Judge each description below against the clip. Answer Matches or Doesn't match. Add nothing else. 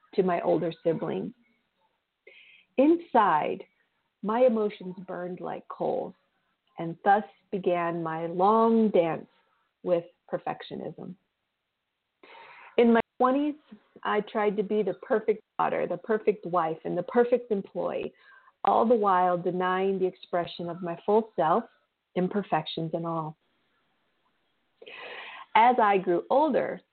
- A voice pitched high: Matches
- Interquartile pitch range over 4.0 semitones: Matches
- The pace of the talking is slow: Matches